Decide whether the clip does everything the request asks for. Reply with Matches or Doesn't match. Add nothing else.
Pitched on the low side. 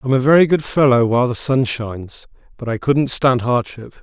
Matches